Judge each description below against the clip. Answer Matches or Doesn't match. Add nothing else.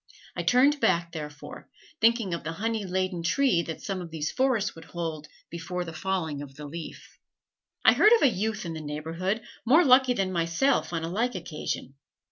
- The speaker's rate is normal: Matches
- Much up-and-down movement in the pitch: Matches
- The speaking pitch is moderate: Matches